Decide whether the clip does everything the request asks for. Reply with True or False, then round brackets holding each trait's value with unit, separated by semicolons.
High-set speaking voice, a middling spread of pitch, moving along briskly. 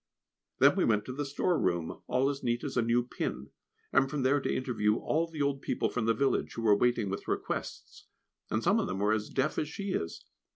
False (125 Hz; 4.5 semitones; 225 wpm)